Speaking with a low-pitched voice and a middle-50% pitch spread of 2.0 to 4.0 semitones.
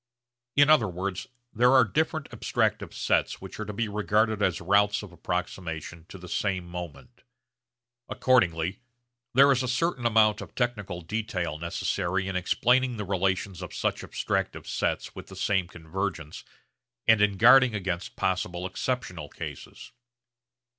No: low, 100 Hz; average, 4.6 semitones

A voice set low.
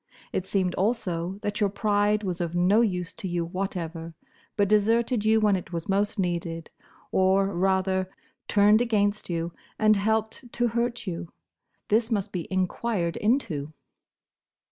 No: high, 195 Hz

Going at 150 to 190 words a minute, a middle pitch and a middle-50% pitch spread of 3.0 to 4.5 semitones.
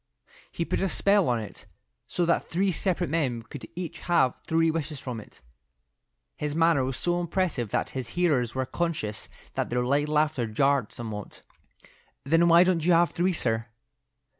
No: average, 170 wpm; medium, 155 Hz; wide, 5.5 semitones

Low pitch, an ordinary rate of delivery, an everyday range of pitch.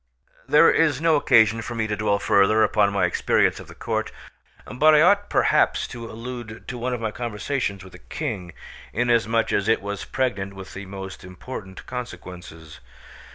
Yes: low, 110 Hz; average, 175 wpm; average, 4.1 semitones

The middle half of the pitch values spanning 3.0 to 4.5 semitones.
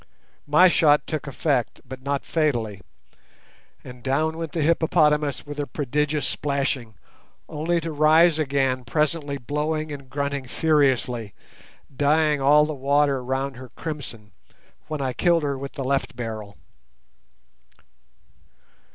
No: narrow, 2.6 semitones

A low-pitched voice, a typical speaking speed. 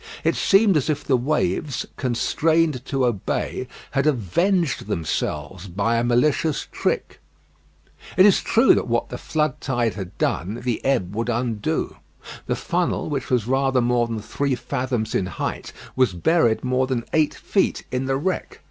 Yes: low, 125 Hz; average, 160 wpm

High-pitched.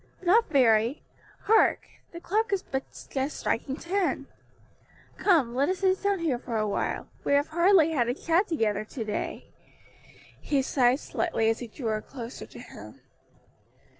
Yes: very high, 280 Hz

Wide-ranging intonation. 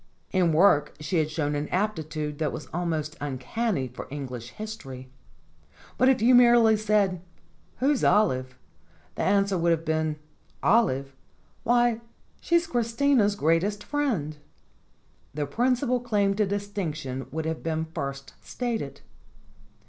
Yes: wide, 6.9 semitones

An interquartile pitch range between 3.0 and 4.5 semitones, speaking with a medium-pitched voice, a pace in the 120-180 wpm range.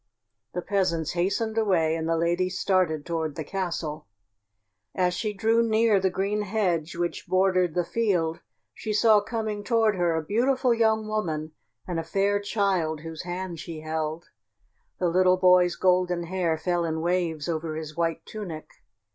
Yes: average, 3.7 semitones; medium, 180 Hz; average, 160 wpm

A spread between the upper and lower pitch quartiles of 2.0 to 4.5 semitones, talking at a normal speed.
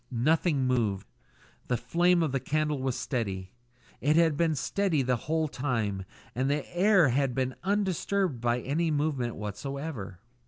No: average, 5.0 semitones; average, 150 wpm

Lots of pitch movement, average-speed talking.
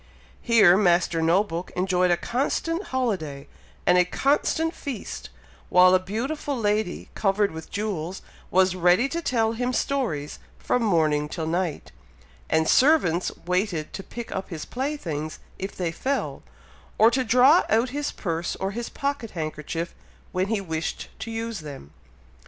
Yes: wide, 6.1 semitones; average, 150 wpm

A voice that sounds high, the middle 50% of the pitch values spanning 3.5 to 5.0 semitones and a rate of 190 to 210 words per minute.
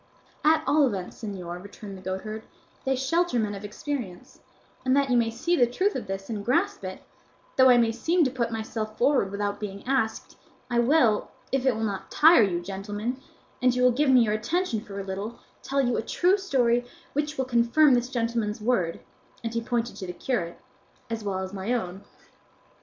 Yes: high, 235 Hz; average, 4.4 semitones; average, 200 wpm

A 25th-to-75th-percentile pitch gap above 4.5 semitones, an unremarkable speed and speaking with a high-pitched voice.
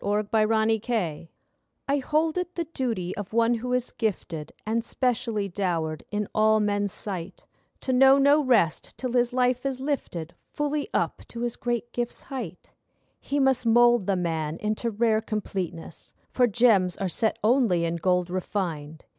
Yes: average, 5.2 semitones; average, 160 wpm; high, 220 Hz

